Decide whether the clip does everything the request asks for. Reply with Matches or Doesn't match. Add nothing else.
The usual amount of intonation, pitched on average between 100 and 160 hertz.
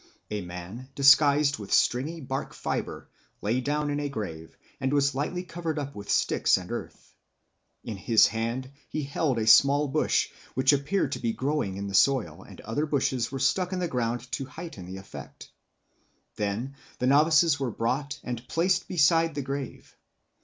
Matches